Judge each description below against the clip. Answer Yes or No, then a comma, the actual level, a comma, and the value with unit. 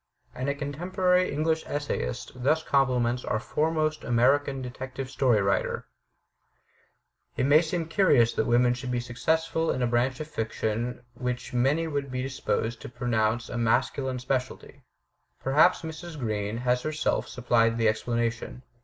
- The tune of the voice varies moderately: Yes, average, 4.0 semitones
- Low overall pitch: Yes, low, 130 Hz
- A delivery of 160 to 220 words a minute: No, average, 145 wpm